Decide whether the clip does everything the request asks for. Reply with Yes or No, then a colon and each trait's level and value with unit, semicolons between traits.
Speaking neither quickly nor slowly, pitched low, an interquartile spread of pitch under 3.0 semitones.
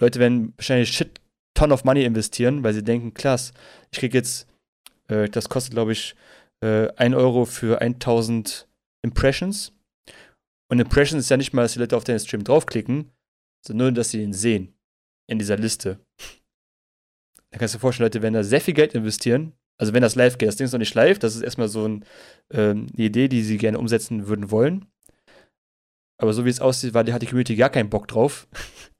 No: fast, 205 wpm; low, 120 Hz; narrow, 2.5 semitones